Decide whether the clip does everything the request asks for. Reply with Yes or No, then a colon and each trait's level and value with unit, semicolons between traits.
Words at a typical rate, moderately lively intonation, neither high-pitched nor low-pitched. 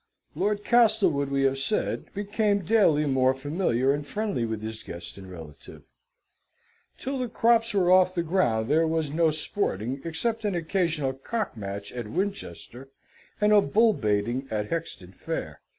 No: average, 155 wpm; wide, 8.8 semitones; medium, 155 Hz